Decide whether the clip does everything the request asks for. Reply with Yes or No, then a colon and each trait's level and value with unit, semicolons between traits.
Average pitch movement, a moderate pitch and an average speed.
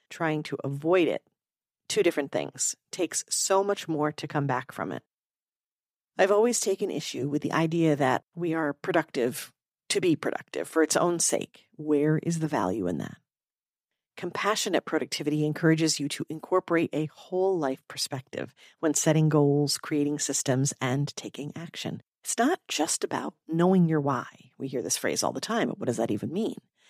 Yes: average, 3.0 semitones; medium, 155 Hz; average, 175 wpm